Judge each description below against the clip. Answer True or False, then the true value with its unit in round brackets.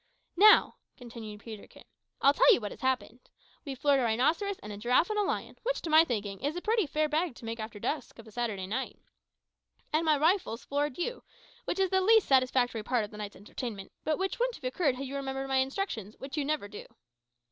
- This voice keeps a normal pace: False (230 wpm)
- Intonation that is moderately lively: False (6.1 semitones)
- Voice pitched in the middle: False (270 Hz)